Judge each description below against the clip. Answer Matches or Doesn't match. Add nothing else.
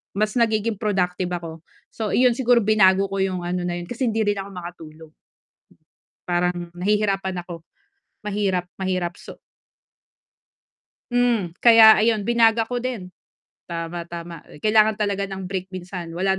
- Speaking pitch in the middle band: Doesn't match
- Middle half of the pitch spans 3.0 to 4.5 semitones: Matches